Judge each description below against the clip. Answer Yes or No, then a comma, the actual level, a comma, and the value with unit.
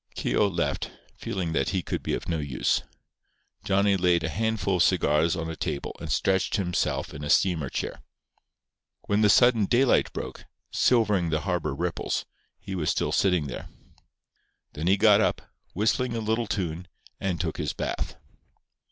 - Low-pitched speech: Yes, very low, 95 Hz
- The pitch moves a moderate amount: Yes, average, 4.0 semitones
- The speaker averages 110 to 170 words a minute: Yes, average, 165 wpm